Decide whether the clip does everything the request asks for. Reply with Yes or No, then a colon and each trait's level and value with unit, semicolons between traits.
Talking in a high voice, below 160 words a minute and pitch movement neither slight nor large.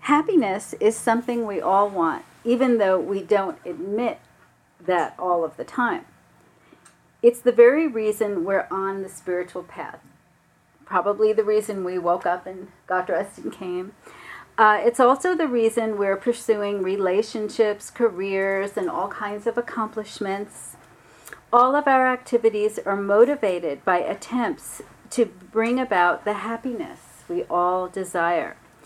Yes: high, 210 Hz; slow, 135 wpm; average, 3.9 semitones